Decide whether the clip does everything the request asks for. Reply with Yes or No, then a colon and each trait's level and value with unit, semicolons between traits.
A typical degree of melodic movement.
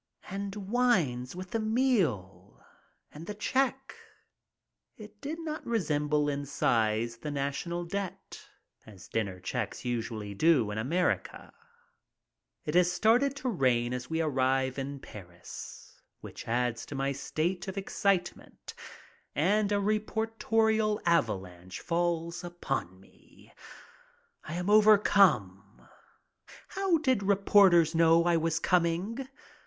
No: wide, 8.6 semitones